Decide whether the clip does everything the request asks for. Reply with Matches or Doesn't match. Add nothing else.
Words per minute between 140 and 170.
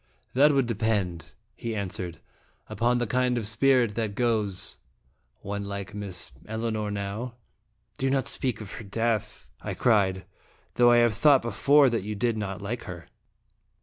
Matches